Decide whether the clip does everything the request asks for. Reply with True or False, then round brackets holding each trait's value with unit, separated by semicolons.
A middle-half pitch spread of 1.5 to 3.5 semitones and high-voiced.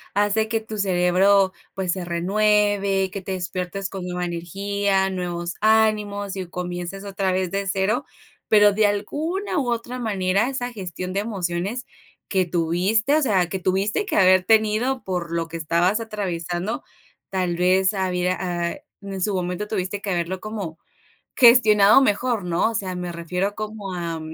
True (2.9 semitones; 195 Hz)